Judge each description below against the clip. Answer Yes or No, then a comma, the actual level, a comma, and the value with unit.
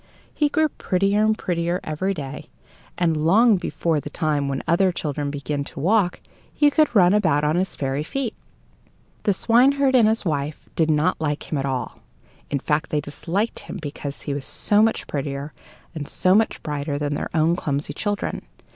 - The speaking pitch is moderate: Yes, medium, 165 Hz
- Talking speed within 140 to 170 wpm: No, average, 180 wpm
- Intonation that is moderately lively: No, wide, 5.9 semitones